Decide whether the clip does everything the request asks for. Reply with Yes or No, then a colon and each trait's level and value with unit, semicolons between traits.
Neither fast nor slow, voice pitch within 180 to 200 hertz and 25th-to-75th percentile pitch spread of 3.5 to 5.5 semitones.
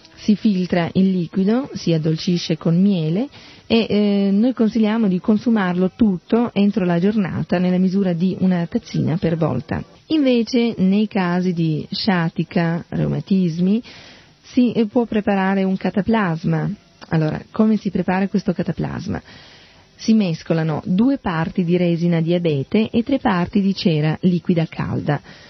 Yes: average, 130 wpm; high, 190 Hz; average, 3.8 semitones